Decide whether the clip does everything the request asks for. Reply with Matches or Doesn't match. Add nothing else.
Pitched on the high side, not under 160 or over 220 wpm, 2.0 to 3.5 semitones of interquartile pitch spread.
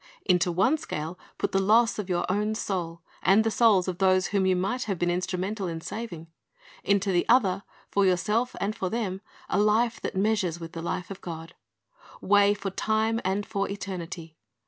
Matches